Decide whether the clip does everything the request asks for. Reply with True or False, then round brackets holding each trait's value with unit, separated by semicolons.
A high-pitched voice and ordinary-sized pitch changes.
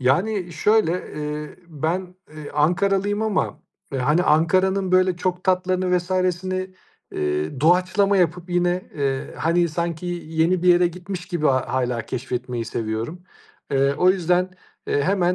False (175 Hz; 3.6 semitones)